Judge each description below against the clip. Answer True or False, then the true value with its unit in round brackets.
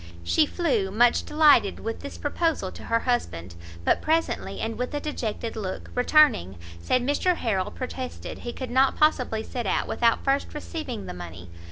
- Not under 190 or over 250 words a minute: False (170 wpm)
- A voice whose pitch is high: True (245 Hz)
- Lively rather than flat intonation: True (5.8 semitones)